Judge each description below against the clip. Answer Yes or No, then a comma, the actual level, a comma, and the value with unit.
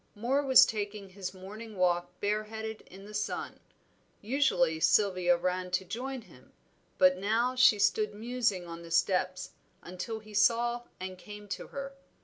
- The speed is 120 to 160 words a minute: Yes, average, 150 wpm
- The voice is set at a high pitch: Yes, high, 205 Hz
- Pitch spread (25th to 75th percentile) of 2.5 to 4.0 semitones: Yes, average, 3.7 semitones